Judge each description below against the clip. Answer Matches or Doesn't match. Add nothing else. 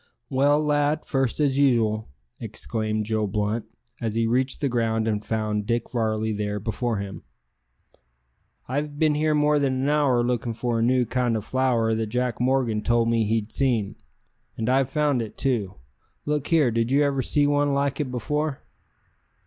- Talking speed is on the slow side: Doesn't match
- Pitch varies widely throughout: Doesn't match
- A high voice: Doesn't match